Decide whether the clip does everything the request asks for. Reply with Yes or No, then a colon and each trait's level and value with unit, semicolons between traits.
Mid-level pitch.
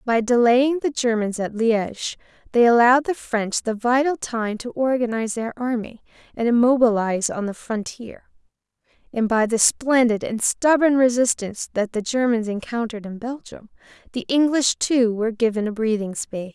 No: high, 235 Hz